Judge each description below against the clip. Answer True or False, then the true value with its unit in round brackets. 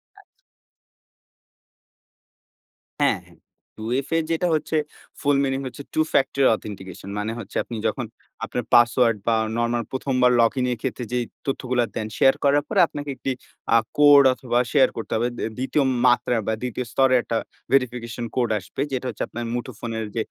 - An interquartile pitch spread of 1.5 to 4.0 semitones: True (2.6 semitones)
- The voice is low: True (125 Hz)